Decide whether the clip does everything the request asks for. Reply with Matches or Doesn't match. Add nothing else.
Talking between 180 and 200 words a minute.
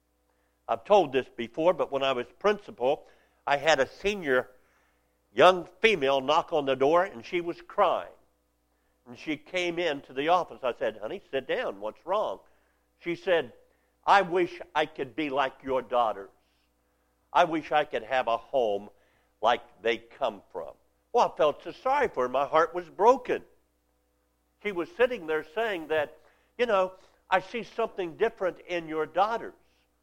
Doesn't match